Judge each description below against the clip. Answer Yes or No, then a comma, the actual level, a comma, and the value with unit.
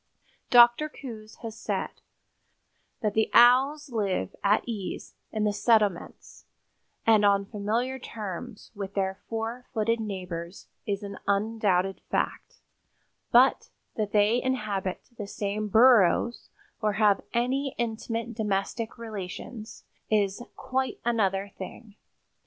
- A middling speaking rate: No, slow, 115 wpm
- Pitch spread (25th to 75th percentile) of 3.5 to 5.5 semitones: No, average, 2.9 semitones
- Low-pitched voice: No, high, 215 Hz